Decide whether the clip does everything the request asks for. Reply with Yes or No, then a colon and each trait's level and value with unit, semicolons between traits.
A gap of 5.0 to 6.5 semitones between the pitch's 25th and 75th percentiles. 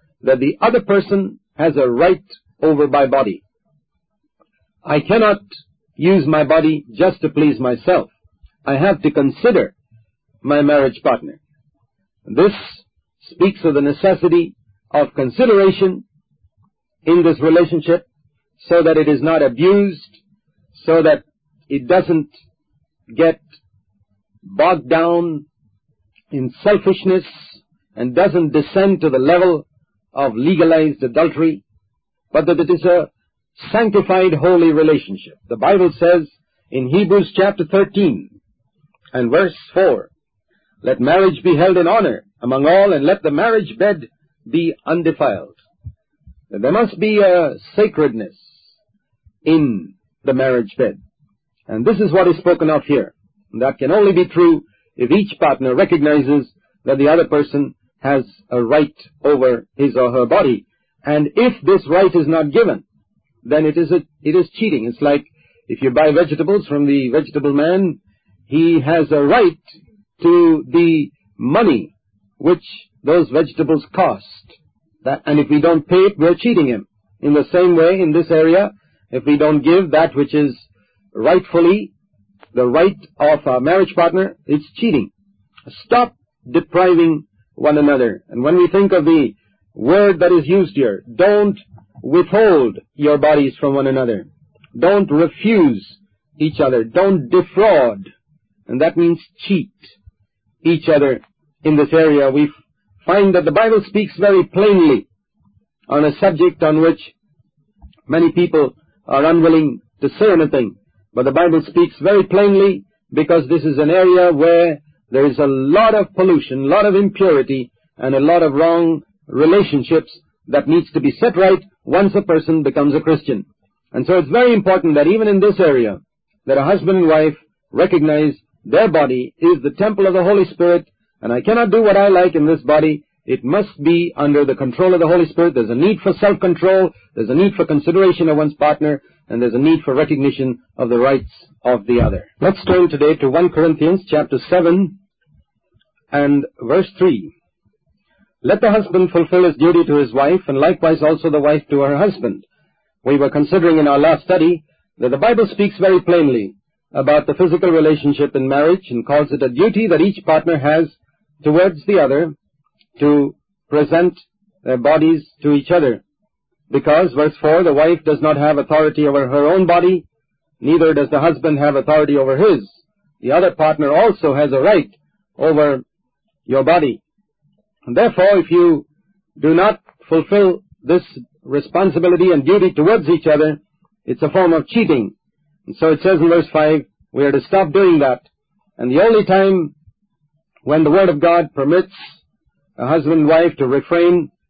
No: average, 4.3 semitones